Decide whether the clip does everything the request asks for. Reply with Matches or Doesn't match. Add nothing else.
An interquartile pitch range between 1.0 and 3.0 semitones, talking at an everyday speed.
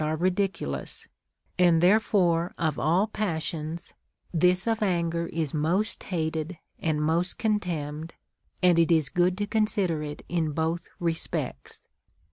Doesn't match